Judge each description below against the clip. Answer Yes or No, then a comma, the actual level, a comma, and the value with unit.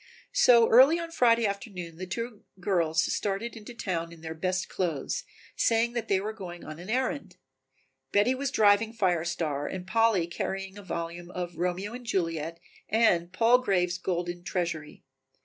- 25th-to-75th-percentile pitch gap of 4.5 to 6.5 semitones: Yes, average, 4.8 semitones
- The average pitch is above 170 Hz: Yes, high, 190 Hz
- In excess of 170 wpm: No, average, 165 wpm